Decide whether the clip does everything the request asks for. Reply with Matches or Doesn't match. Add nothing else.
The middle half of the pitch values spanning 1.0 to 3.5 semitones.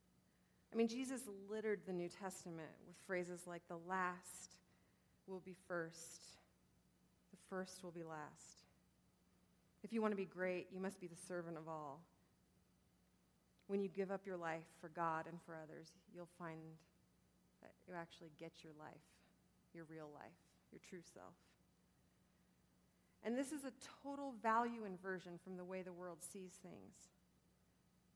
Matches